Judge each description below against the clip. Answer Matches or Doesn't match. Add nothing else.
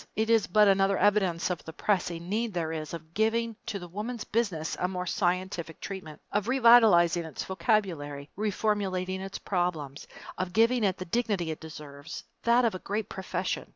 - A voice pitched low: Doesn't match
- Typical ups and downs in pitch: Matches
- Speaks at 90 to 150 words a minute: Doesn't match